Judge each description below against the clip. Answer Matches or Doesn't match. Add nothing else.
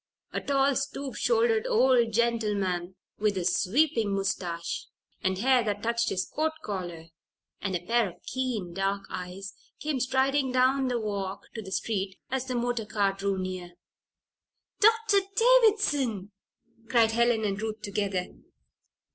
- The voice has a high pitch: Matches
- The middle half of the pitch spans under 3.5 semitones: Doesn't match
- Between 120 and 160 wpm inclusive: Matches